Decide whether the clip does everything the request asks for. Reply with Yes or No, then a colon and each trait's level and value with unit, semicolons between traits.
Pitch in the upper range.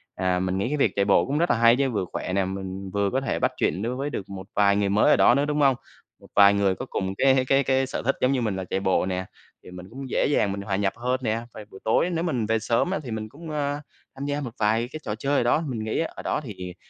No: low, 115 Hz